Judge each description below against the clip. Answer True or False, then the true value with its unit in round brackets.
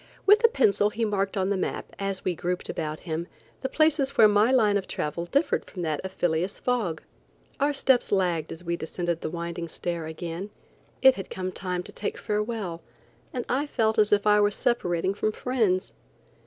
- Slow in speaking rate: False (195 wpm)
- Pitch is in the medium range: False (195 Hz)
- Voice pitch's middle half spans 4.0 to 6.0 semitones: True (4.4 semitones)